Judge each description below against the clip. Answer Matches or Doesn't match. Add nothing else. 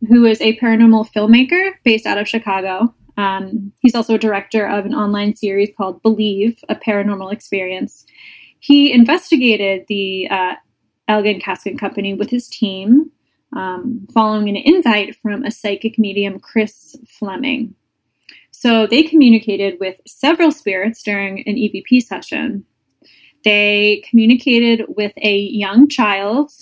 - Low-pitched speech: Doesn't match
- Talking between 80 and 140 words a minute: Matches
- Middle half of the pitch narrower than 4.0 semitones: Matches